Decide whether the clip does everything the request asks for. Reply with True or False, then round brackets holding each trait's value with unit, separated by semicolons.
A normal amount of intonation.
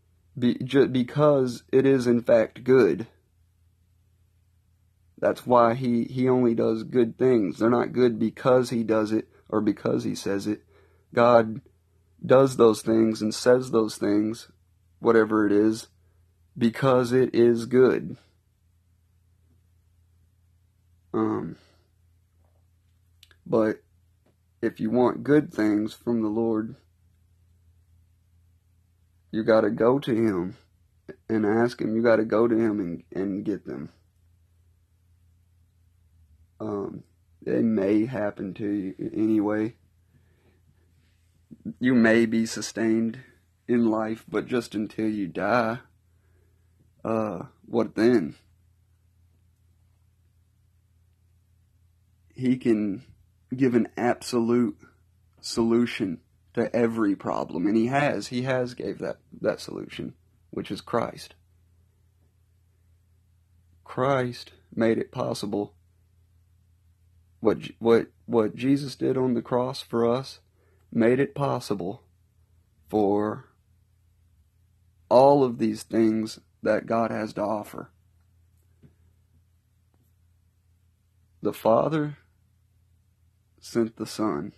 True (4.4 semitones)